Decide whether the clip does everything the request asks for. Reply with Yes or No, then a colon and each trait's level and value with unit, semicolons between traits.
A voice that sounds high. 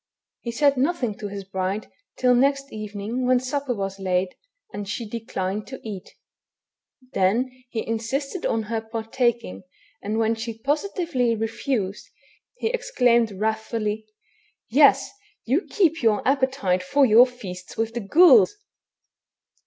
Yes: high, 230 Hz